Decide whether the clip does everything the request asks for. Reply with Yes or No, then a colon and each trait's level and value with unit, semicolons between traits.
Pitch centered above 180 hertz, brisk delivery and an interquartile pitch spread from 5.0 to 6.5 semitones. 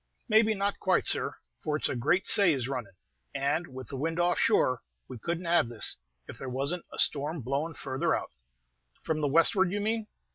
No: medium, 155 Hz; fast, 210 wpm; average, 5.3 semitones